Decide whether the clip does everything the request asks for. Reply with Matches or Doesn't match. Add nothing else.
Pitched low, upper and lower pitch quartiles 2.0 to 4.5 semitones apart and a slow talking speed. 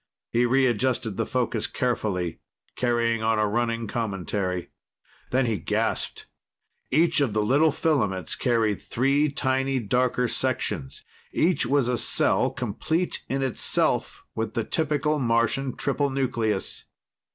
Matches